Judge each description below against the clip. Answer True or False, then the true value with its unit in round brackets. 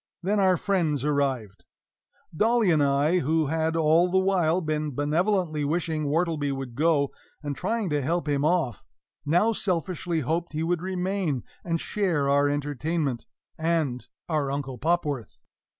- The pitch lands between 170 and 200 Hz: False (160 Hz)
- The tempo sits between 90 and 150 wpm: True (145 wpm)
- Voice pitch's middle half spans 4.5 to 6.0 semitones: False (3.6 semitones)